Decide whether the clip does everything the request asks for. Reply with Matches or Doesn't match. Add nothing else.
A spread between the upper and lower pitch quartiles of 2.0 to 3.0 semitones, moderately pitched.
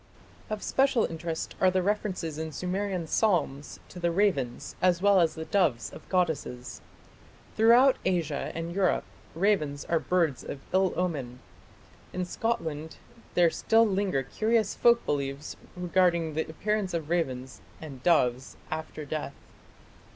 Doesn't match